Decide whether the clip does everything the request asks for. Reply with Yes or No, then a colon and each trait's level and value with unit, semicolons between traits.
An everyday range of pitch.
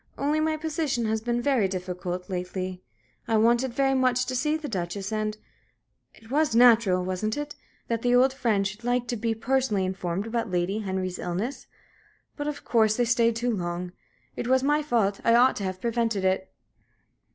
Yes: average, 4.9 semitones